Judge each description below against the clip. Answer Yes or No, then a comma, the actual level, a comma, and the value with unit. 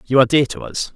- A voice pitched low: Yes, low, 120 Hz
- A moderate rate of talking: No, fast, 315 wpm